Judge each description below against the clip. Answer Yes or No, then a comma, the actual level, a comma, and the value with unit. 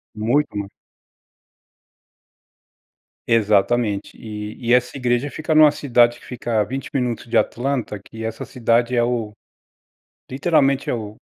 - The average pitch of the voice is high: No, low, 120 Hz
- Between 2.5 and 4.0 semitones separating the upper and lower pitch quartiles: Yes, average, 2.9 semitones